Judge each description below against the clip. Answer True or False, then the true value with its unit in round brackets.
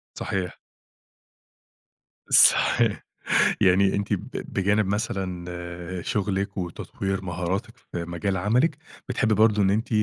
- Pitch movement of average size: False (2.2 semitones)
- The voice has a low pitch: True (100 Hz)